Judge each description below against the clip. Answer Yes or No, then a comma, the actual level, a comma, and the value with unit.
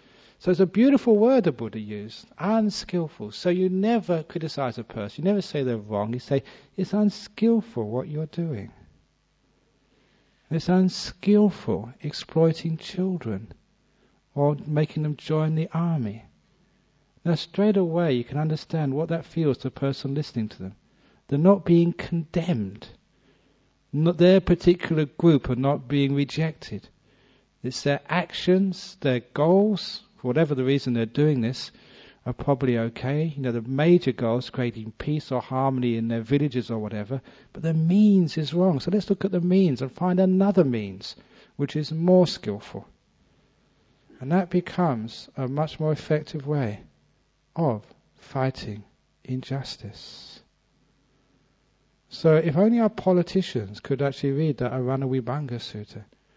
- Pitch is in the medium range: Yes, medium, 150 Hz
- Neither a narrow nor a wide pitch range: No, wide, 6.1 semitones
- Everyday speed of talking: Yes, average, 145 wpm